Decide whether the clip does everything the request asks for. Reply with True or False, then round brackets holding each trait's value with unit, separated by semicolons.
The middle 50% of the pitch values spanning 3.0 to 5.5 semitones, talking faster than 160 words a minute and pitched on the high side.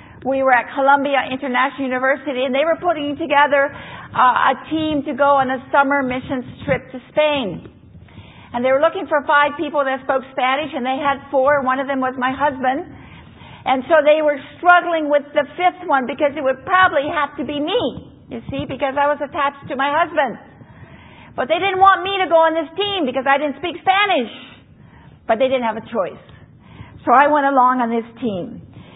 False (2.4 semitones; 200 wpm; 280 Hz)